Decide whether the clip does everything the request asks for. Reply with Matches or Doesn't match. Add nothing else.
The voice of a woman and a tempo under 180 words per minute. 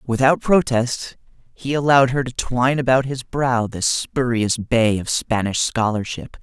Doesn't match